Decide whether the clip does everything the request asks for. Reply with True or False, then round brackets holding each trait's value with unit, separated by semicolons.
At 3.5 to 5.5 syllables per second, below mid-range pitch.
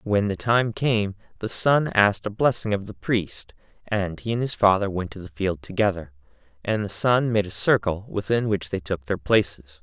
True (4.9 syllables/s; 100 Hz)